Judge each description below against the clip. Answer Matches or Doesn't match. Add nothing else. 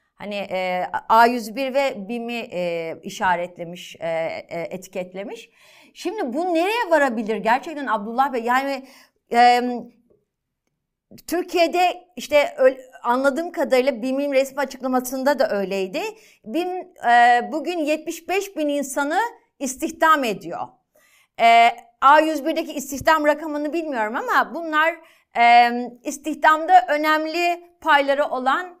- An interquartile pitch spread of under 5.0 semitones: Doesn't match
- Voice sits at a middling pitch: Doesn't match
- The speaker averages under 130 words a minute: Matches